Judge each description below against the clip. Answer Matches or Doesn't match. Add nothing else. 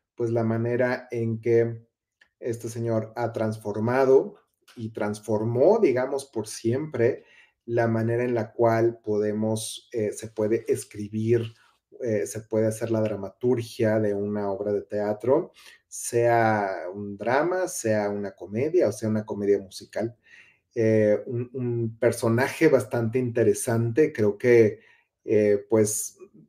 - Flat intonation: Matches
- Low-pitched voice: Matches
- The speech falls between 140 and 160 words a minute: Doesn't match